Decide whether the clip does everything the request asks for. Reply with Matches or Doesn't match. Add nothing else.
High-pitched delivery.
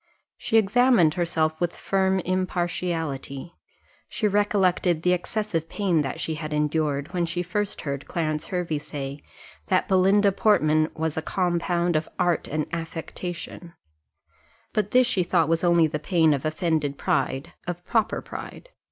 Doesn't match